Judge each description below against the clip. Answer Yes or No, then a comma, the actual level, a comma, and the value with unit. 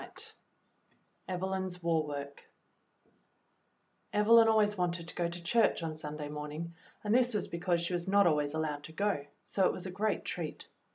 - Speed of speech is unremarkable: Yes, average, 180 wpm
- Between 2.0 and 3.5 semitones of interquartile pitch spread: No, average, 4.3 semitones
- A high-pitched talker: No, medium, 175 Hz